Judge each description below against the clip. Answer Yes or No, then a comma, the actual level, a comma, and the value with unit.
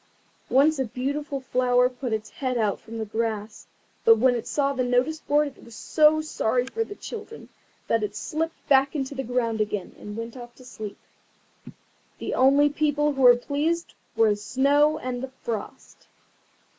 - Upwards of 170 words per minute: Yes, average, 180 wpm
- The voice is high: Yes, very high, 255 Hz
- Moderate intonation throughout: Yes, average, 4.2 semitones